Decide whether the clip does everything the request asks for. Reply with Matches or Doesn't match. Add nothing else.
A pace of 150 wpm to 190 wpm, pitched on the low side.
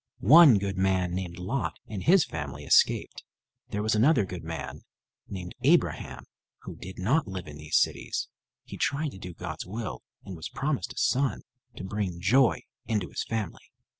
Matches